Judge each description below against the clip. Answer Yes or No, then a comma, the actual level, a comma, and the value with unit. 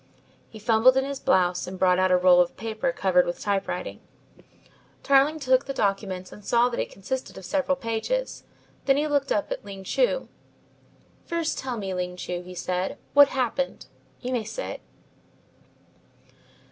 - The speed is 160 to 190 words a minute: Yes, average, 165 wpm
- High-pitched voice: Yes, high, 225 Hz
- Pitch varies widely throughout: Yes, wide, 6.5 semitones